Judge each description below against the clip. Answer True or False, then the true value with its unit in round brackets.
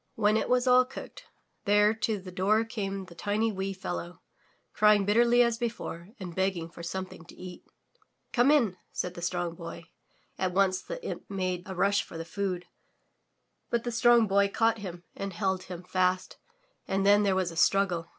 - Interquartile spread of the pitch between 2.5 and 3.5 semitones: True (3.2 semitones)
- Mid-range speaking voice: False (195 Hz)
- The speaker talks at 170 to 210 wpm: True (180 wpm)